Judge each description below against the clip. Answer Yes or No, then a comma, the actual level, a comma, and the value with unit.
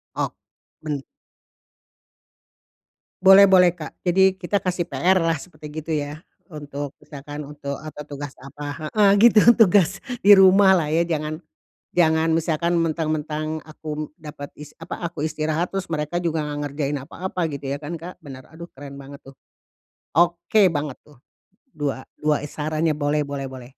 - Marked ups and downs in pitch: No, average, 2.9 semitones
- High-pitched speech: No, medium, 155 Hz